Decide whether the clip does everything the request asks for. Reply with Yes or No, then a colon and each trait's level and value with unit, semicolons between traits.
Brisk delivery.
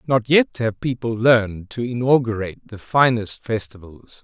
No: average, 140 wpm